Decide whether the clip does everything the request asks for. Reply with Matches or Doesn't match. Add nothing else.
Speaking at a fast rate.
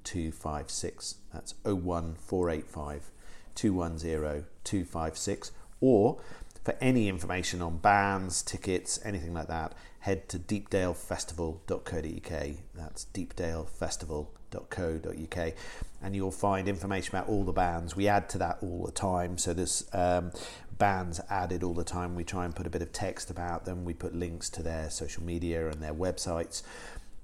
Doesn't match